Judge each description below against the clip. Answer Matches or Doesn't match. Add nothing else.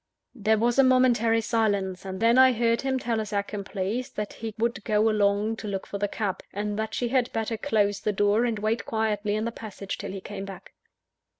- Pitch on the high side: Matches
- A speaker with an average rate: Doesn't match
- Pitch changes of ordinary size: Doesn't match